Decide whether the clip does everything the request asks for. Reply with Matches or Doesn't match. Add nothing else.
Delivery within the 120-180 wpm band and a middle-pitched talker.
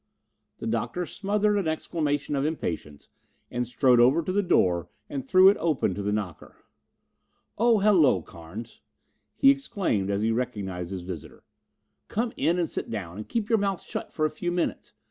Matches